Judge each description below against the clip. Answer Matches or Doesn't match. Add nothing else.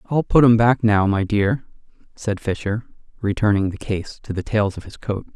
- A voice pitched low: Matches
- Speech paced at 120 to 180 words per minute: Doesn't match